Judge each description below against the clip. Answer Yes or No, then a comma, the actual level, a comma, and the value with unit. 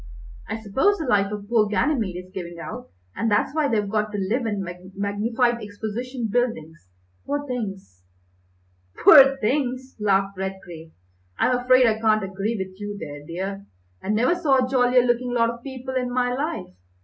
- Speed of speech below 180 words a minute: Yes, average, 170 wpm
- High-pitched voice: Yes, high, 220 Hz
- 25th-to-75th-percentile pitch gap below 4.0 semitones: No, average, 4.3 semitones